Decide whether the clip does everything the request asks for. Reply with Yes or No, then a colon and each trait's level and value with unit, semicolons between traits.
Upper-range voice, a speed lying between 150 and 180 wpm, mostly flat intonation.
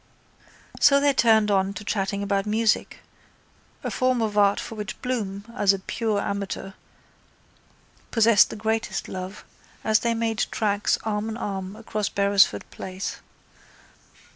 No: high, 210 Hz; average, 140 wpm; narrow, 2.1 semitones